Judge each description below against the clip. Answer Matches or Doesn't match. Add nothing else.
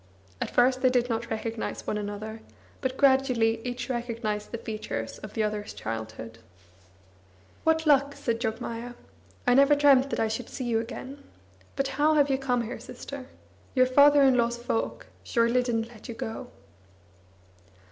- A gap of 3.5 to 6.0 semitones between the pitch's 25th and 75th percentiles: Doesn't match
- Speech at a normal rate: Matches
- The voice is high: Matches